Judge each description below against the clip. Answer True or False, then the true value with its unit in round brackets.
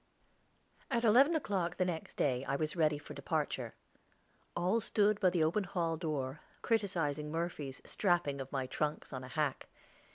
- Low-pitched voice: False (165 Hz)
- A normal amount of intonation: True (4.8 semitones)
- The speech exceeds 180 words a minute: False (160 wpm)